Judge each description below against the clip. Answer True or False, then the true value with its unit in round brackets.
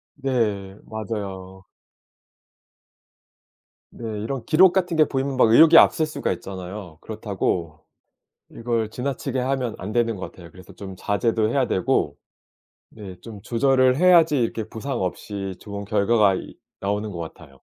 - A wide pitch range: False (4.9 semitones)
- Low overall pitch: True (110 Hz)